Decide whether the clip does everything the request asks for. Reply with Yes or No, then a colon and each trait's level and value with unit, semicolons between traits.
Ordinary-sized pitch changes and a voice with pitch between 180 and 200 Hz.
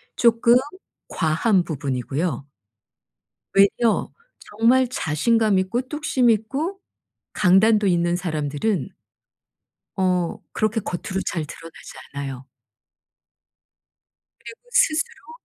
No: wide, 6.1 semitones; high, 190 Hz